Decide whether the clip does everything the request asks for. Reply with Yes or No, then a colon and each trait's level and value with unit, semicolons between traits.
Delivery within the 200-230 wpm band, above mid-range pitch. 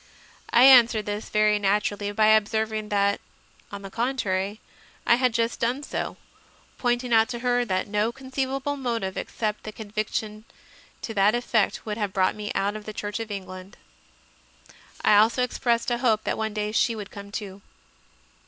No: average, 170 wpm; high, 215 Hz